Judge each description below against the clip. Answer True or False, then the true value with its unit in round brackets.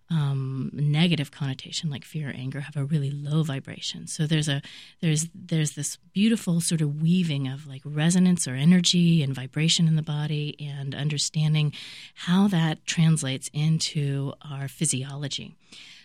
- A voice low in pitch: False (150 Hz)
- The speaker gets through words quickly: False (150 wpm)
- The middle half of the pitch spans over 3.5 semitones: False (2.8 semitones)